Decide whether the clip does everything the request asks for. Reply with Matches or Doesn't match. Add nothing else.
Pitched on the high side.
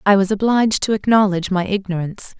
Matches